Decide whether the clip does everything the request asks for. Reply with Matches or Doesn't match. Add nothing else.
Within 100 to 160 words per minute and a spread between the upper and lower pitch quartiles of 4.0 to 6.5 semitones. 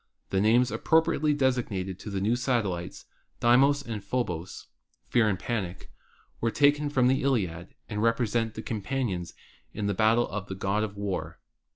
Matches